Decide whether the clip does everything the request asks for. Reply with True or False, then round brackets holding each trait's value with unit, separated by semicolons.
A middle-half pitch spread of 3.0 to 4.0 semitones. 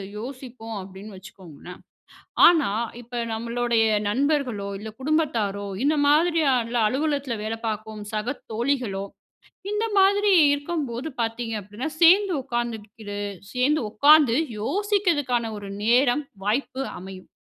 False (5.1 semitones)